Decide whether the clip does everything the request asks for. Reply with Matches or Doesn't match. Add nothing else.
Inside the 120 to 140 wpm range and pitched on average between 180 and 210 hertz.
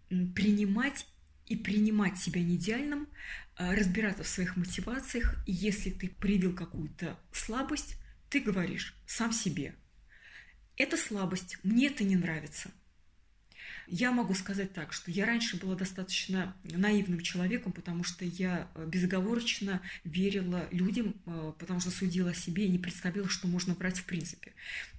Matches